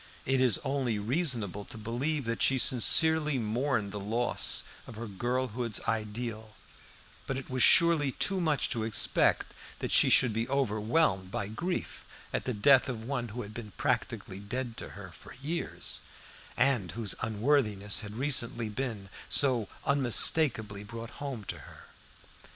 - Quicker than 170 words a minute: No, average, 150 wpm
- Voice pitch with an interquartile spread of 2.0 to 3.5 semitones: No, average, 4.1 semitones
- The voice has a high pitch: No, low, 120 Hz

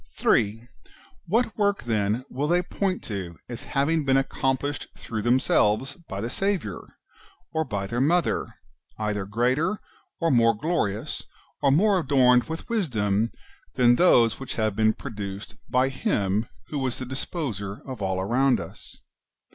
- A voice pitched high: No, low, 125 Hz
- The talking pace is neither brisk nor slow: Yes, average, 145 wpm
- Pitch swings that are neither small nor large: No, wide, 5.8 semitones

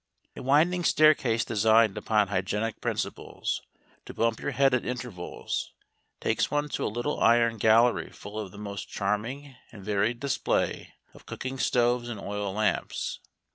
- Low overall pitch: Yes, low, 115 Hz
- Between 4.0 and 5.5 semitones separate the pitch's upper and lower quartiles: No, average, 3.4 semitones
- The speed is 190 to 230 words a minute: No, average, 150 wpm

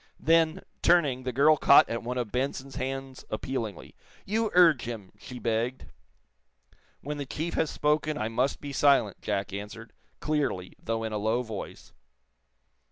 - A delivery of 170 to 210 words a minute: No, average, 155 wpm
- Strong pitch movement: No, average, 4.6 semitones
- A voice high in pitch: No, low, 130 Hz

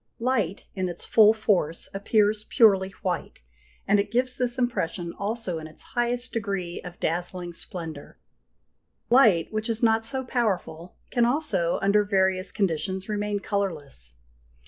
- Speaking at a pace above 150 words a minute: No, average, 140 wpm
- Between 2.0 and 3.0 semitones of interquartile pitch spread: No, average, 4.2 semitones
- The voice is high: Yes, high, 200 Hz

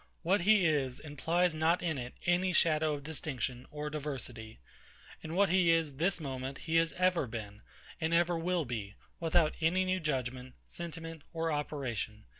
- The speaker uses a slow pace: No, average, 165 wpm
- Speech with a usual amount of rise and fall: Yes, average, 4.5 semitones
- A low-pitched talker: No, medium, 155 Hz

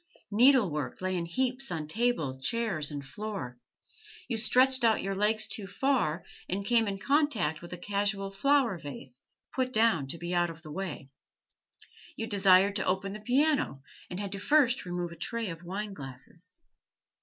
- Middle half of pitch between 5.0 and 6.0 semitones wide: Yes, wide, 5.5 semitones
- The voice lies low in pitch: No, high, 195 Hz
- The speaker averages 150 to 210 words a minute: Yes, average, 165 wpm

